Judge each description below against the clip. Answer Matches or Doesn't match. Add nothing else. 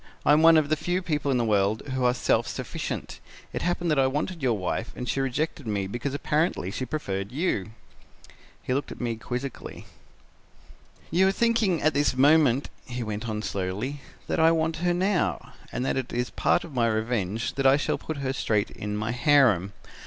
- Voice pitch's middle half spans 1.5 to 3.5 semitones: Doesn't match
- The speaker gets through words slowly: Doesn't match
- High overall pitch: Doesn't match